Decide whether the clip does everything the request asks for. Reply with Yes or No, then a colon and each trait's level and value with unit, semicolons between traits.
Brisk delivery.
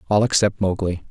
No: average, 165 wpm